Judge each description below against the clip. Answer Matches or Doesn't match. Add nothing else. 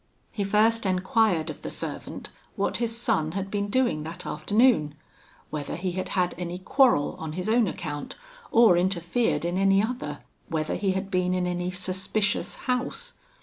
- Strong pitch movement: Doesn't match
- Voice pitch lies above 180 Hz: Matches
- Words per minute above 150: Matches